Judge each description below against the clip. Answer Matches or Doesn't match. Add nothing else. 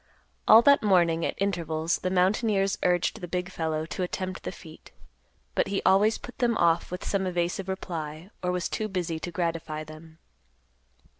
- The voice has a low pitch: Doesn't match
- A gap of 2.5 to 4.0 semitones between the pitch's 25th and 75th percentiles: Matches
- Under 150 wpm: Doesn't match